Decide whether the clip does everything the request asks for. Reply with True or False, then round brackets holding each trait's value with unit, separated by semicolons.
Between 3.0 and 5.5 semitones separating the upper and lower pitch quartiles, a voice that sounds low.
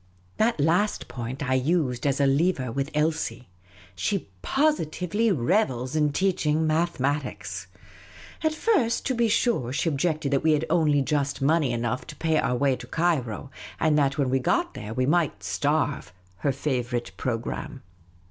False (4.5 semitones; 145 Hz)